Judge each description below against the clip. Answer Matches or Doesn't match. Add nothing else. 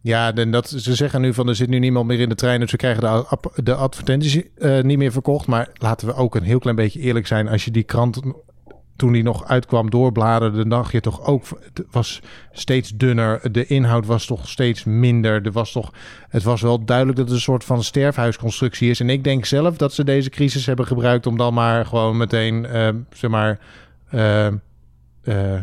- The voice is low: Matches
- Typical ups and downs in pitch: Doesn't match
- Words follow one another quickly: Matches